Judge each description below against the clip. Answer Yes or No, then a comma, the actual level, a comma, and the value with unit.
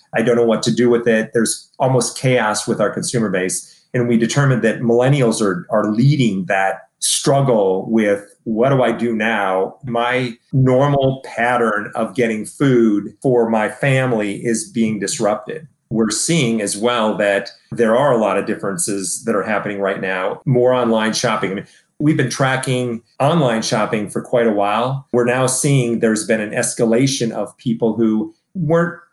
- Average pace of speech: Yes, average, 175 wpm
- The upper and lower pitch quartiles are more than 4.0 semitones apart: No, average, 2.8 semitones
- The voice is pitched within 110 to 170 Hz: Yes, low, 115 Hz